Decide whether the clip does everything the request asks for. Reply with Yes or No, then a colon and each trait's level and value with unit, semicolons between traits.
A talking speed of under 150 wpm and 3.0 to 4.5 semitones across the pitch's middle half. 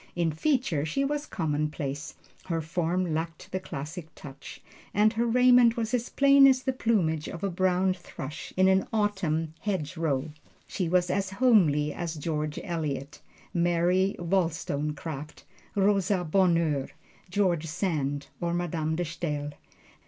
Yes: slow, 135 wpm; average, 4.1 semitones